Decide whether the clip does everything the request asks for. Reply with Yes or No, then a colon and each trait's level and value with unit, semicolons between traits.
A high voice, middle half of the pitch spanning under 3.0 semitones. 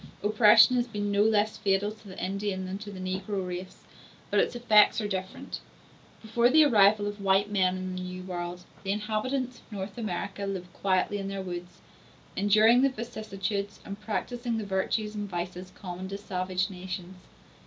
Yes: high, 200 Hz; narrow, 2.4 semitones